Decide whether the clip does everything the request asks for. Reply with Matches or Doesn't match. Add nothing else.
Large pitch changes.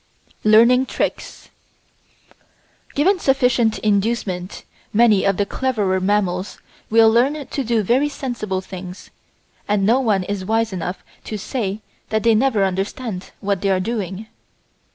Doesn't match